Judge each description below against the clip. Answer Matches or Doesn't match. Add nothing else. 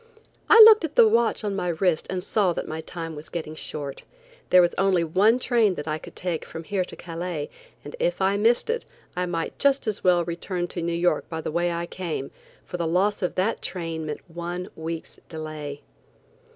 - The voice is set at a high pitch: Doesn't match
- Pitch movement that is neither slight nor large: Matches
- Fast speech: Matches